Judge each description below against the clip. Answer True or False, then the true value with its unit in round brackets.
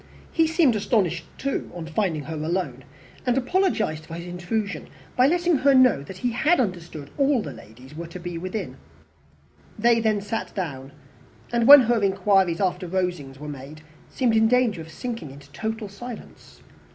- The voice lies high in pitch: True (195 Hz)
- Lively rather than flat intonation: True (6.8 semitones)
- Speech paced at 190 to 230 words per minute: False (165 wpm)